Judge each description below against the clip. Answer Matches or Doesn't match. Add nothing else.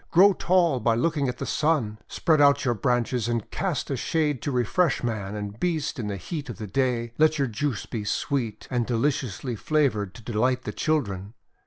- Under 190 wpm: Doesn't match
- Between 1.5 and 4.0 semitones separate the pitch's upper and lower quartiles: Doesn't match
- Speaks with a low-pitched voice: Matches